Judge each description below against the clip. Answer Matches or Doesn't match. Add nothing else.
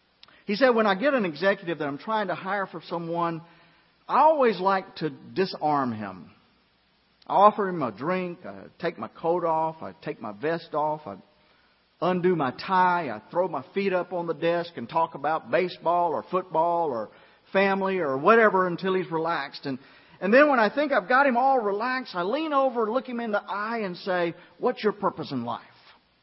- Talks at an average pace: Matches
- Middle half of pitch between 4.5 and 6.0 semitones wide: Doesn't match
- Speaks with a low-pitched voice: Doesn't match